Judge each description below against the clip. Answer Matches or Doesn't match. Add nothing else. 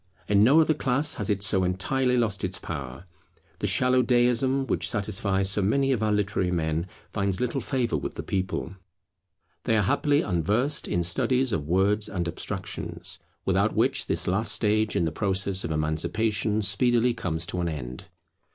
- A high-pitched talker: Doesn't match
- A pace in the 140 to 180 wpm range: Matches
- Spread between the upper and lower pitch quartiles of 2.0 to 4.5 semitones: Doesn't match